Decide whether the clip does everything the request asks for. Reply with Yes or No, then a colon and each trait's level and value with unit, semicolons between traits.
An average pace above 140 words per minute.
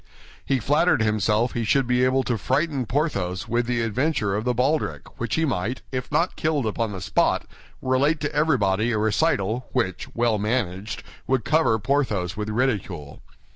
Yes: average, 170 wpm